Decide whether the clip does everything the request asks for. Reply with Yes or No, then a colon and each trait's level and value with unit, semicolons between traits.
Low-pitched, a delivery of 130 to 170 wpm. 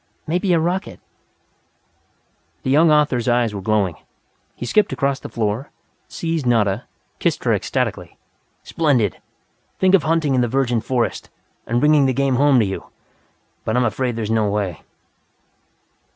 Yes: low, 125 Hz; average, 155 wpm